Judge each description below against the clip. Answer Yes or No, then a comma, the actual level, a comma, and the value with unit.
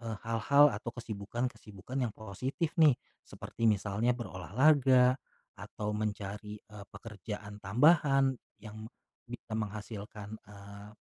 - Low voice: Yes, low, 110 Hz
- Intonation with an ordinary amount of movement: Yes, average, 3.2 semitones